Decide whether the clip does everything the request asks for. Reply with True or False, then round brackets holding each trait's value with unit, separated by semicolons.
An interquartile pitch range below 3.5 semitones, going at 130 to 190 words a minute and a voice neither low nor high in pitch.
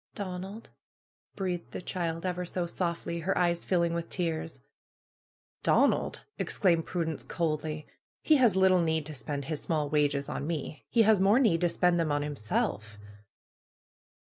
True (3.0 semitones; 160 wpm; 170 Hz)